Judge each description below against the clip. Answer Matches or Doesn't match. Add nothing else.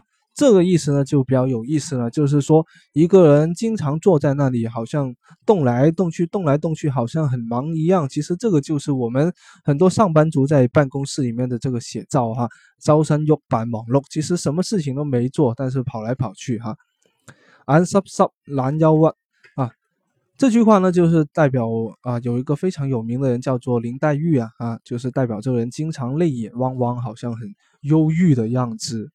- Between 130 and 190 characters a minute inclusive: Doesn't match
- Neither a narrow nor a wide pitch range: Matches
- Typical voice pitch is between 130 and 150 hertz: Matches